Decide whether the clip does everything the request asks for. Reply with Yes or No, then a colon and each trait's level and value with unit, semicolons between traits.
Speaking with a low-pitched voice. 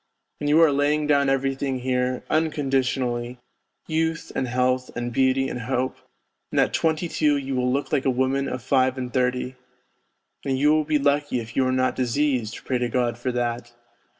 Yes: low, 130 Hz